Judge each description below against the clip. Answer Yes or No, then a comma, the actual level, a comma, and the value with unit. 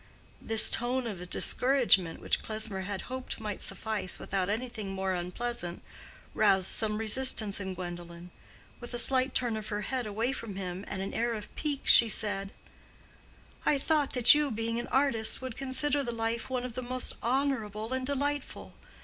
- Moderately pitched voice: No, high, 225 Hz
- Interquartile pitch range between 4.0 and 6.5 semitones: Yes, average, 4.6 semitones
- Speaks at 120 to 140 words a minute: No, average, 170 wpm